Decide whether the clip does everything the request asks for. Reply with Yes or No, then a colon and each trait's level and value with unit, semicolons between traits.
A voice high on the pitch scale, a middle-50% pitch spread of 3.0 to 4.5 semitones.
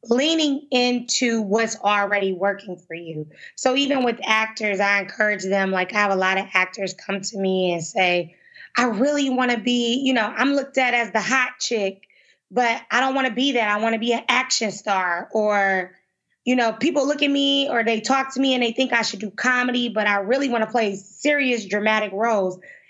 Yes: high, 225 Hz; average, 4.1 semitones